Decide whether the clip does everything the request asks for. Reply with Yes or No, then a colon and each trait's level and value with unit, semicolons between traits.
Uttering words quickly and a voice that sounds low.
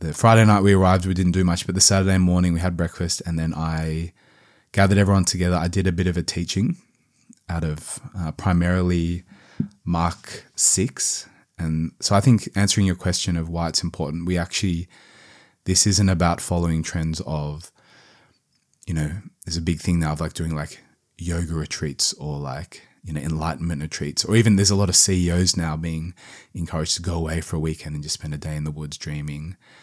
No: average, 195 wpm; very low, 85 Hz